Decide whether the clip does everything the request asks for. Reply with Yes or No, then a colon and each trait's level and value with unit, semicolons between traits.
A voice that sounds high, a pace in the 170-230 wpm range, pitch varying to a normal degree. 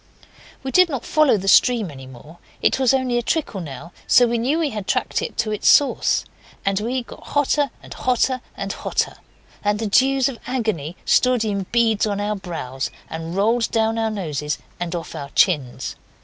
No: high, 220 Hz; average, 190 wpm; wide, 6.0 semitones